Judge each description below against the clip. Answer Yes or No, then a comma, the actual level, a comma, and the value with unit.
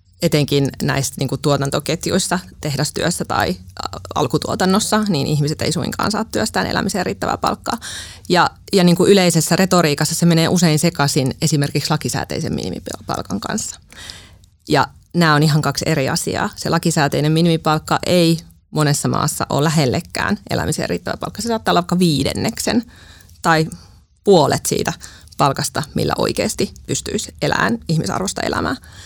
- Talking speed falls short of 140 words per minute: Yes, average, 130 wpm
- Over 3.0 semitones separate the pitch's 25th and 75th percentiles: Yes, average, 3.8 semitones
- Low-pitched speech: No, medium, 155 Hz